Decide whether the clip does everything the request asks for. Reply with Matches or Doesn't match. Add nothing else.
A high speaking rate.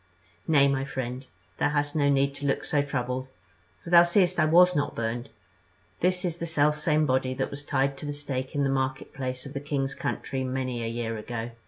Matches